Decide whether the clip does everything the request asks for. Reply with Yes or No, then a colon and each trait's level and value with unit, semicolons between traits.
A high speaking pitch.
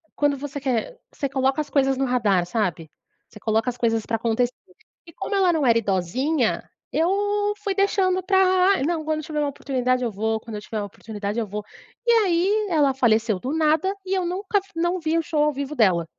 Yes: very high, 280 Hz